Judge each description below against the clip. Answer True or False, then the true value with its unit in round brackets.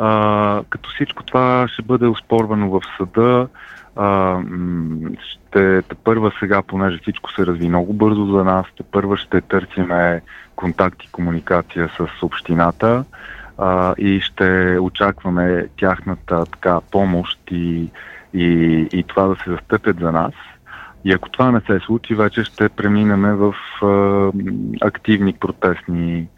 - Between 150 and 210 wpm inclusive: False (135 wpm)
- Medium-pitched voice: False (95 Hz)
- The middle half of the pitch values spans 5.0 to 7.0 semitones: False (3.0 semitones)